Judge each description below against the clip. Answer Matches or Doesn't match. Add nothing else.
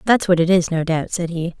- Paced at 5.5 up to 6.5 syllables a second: Matches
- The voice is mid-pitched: Matches